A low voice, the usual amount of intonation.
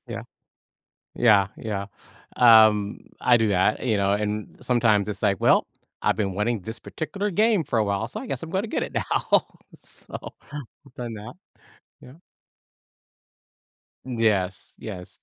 Yes: low, 110 Hz; average, 3.6 semitones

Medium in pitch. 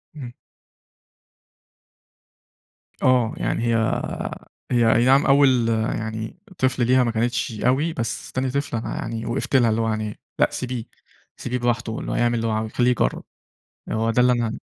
No: low, 120 Hz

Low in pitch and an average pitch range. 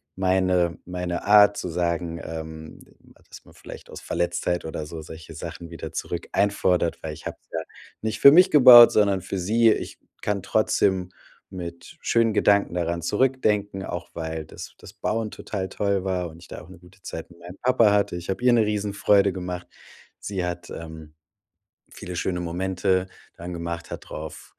Yes: very low, 90 Hz; average, 3.2 semitones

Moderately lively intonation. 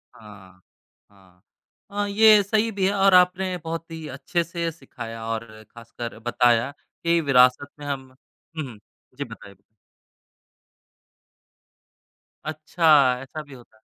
No: wide, 7.0 semitones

